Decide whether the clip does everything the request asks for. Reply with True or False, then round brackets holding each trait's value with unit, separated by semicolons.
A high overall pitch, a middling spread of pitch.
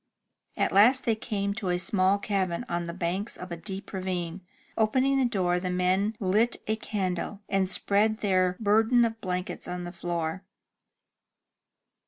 True (195 Hz; 3.1 semitones)